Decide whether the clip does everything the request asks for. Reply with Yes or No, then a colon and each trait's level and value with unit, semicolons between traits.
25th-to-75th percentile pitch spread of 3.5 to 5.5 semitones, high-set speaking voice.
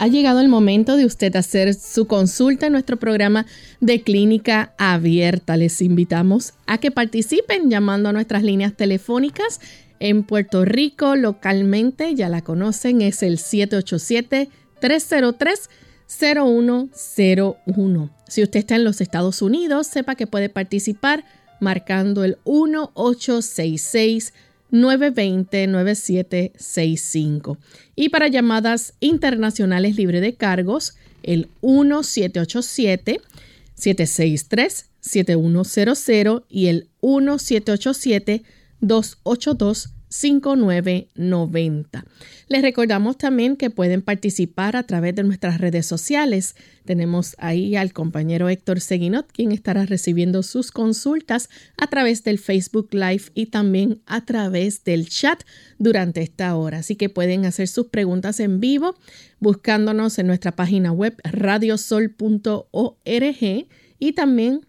Yes: average, 4.6 semitones; high, 210 Hz